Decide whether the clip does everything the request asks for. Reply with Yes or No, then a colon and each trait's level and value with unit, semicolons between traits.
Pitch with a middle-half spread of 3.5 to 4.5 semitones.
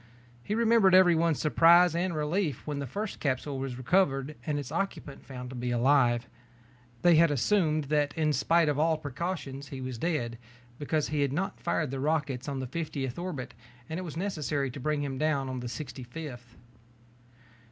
Yes: average, 4.1 semitones